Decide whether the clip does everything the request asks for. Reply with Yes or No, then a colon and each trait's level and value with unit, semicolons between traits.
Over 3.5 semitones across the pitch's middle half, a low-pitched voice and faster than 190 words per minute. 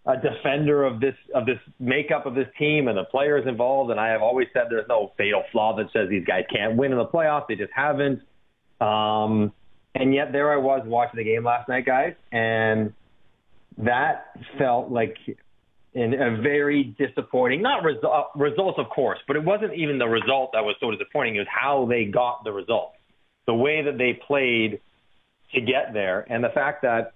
Yes: average, 3.9 semitones; low, 130 Hz; average, 200 wpm